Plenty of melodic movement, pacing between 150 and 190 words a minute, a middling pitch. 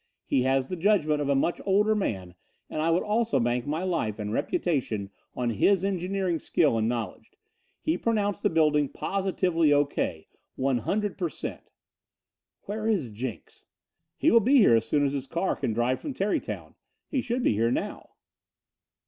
Yes: wide, 8.0 semitones; average, 175 wpm; medium, 155 Hz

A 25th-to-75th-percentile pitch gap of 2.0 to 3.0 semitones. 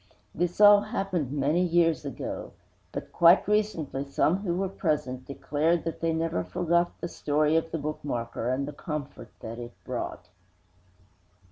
No: average, 3.8 semitones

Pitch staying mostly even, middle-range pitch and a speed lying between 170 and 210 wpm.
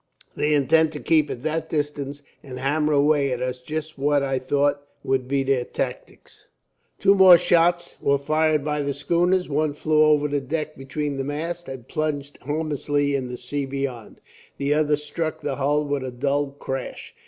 Yes: narrow, 2.0 semitones; medium, 145 Hz; average, 180 wpm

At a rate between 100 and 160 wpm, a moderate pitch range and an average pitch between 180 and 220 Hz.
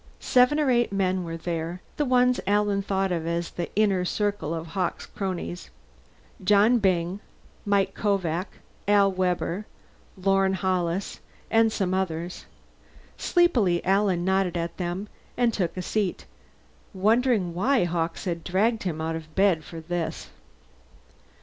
Yes: slow, 135 wpm; average, 3.1 semitones; high, 190 Hz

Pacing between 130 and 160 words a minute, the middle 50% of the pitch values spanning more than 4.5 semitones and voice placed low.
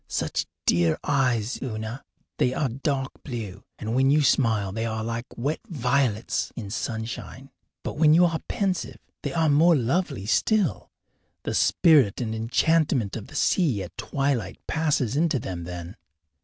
Yes: average, 155 wpm; average, 5.2 semitones; low, 125 Hz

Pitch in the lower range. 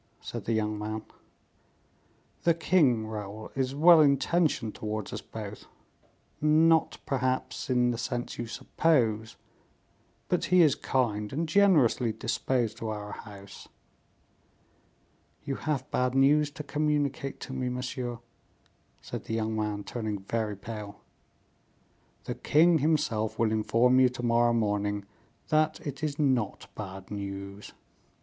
Yes: low, 120 Hz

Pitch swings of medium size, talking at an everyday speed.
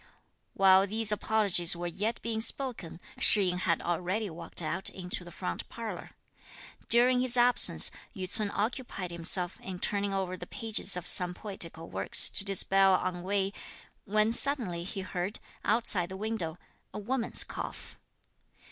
Yes: average, 3.6 semitones; average, 145 wpm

